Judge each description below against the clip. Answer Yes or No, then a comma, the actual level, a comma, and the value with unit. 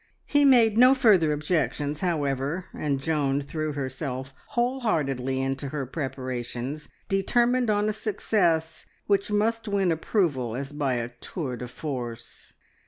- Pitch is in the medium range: Yes, medium, 150 Hz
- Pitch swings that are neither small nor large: No, wide, 7.3 semitones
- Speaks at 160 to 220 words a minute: No, slow, 135 wpm